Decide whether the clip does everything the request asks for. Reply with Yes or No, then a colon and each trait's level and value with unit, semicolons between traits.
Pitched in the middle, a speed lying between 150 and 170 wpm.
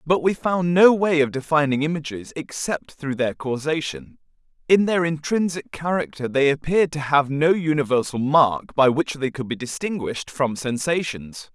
Yes: medium, 150 Hz; average, 160 wpm